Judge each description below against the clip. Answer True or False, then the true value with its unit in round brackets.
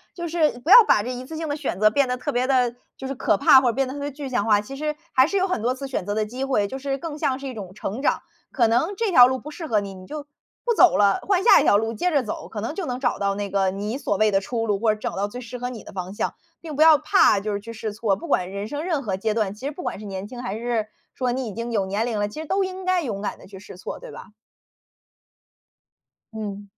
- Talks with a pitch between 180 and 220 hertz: False (240 Hz)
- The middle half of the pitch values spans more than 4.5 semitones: True (5.4 semitones)